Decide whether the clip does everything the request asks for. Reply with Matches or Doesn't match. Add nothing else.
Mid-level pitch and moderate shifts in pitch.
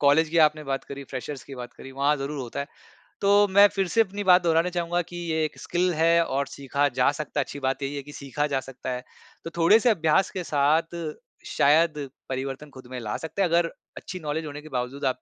Matches